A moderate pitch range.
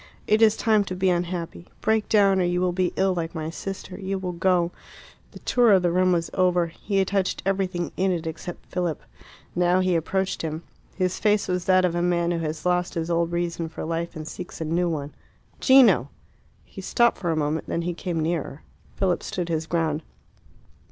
No: narrow, 2.1 semitones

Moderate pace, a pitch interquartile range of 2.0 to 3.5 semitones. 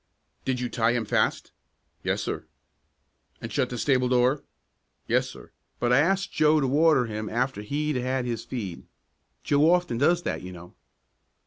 No: average, 165 wpm; average, 4.1 semitones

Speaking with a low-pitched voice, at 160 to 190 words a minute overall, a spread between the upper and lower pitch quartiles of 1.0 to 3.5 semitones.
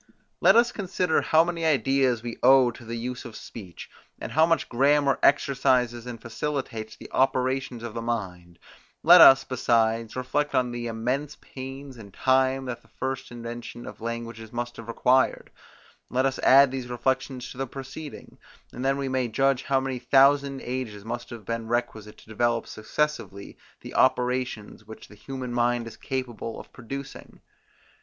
Yes: low, 125 Hz; average, 165 wpm; narrow, 2.5 semitones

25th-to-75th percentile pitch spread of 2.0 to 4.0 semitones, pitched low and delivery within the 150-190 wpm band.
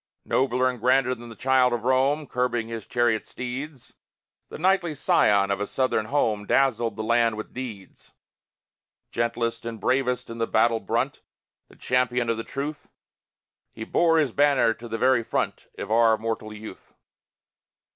Yes: narrow, 2.5 semitones; low, 120 Hz; average, 160 wpm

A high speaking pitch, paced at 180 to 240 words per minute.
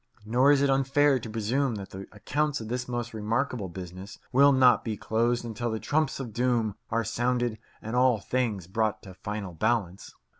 No: low, 115 Hz; average, 185 wpm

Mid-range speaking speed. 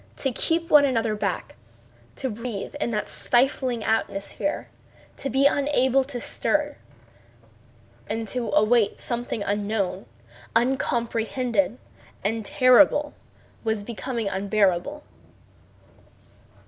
No: slow, 95 wpm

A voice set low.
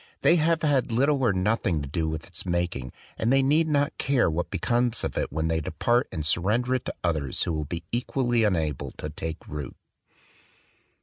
Yes: low, 100 Hz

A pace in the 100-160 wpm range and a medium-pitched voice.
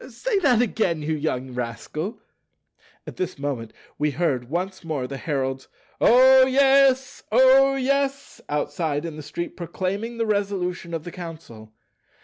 Yes: average, 140 wpm; medium, 175 Hz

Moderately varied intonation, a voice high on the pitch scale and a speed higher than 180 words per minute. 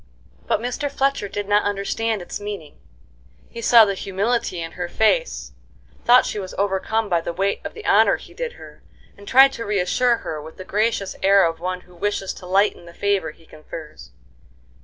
Yes: average, 3.9 semitones; high, 200 Hz; average, 190 wpm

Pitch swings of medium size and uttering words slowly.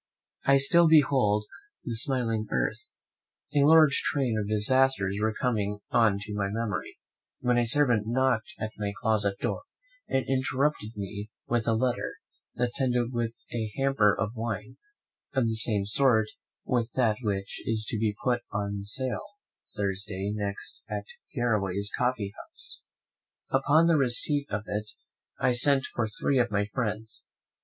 No: average, 3.9 semitones; average, 150 wpm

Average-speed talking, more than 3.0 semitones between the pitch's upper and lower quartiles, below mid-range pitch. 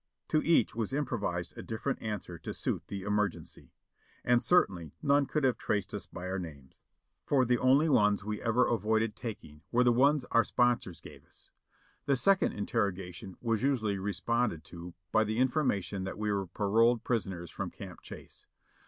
Yes: average, 180 wpm; average, 4.4 semitones; low, 110 Hz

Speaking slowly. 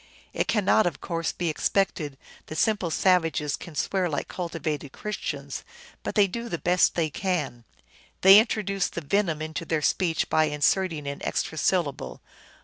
No: average, 155 wpm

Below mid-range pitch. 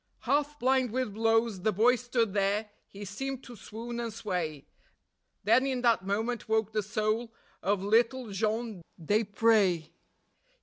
No: high, 220 Hz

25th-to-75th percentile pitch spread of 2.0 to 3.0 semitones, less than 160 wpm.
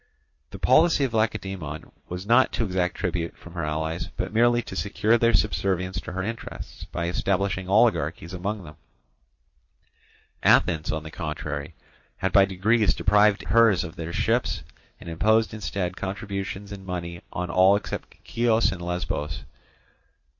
No: average, 3.8 semitones; average, 145 wpm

